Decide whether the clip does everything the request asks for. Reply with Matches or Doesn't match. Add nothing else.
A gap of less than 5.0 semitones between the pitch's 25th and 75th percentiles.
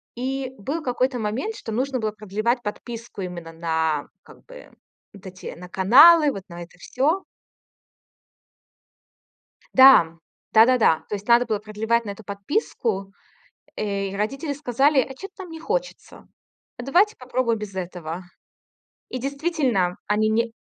Doesn't match